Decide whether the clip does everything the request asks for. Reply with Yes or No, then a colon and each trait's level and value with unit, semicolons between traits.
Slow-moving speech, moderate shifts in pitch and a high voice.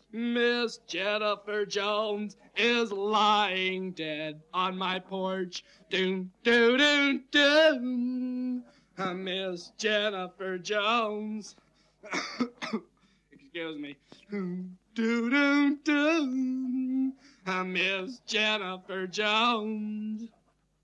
Yes: slow, 75 wpm; average, 4.3 semitones; high, 210 Hz